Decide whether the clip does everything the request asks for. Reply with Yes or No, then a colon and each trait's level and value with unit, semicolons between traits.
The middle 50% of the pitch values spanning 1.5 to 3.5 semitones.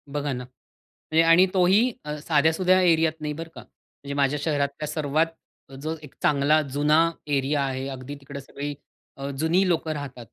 Yes: narrow, 2.5 semitones